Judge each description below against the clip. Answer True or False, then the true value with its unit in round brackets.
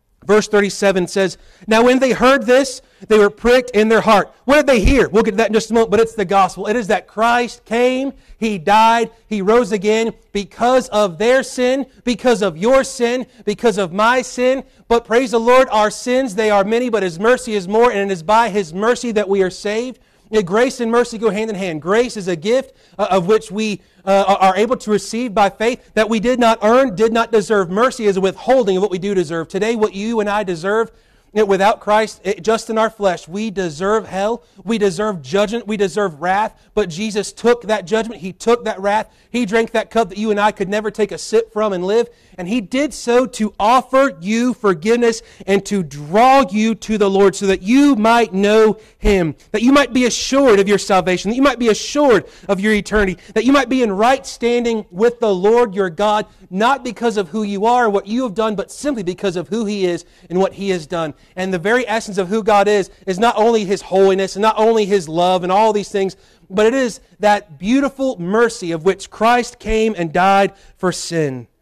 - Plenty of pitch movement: False (3.0 semitones)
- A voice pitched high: True (215 Hz)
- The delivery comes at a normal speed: False (225 wpm)